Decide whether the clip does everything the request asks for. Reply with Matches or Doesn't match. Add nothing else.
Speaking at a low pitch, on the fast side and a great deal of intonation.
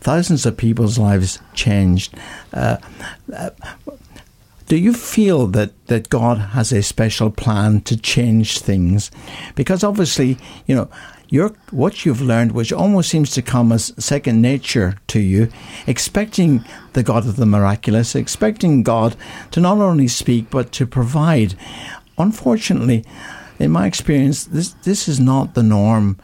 Doesn't match